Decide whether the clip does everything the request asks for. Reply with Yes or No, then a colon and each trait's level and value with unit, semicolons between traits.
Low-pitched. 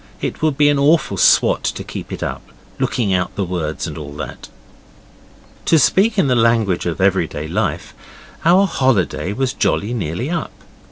Yes: low, 110 Hz